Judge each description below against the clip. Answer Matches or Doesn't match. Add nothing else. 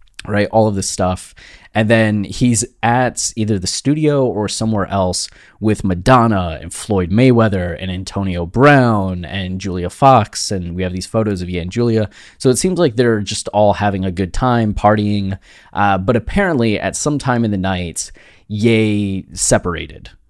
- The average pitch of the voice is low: Matches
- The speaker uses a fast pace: Doesn't match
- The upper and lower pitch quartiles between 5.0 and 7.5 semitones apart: Doesn't match